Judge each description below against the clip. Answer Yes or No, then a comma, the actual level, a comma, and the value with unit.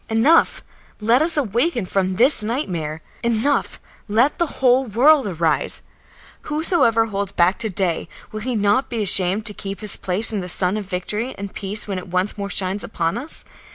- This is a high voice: Yes, high, 210 Hz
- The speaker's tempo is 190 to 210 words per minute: No, average, 180 wpm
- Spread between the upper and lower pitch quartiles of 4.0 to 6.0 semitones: Yes, average, 4.5 semitones